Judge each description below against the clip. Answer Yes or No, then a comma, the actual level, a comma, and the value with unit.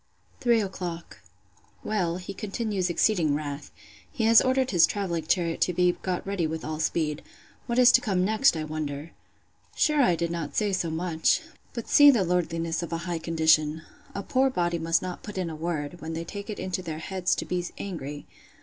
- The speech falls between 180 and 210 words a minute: Yes, average, 190 wpm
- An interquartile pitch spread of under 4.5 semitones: Yes, average, 3.7 semitones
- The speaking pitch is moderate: Yes, medium, 175 Hz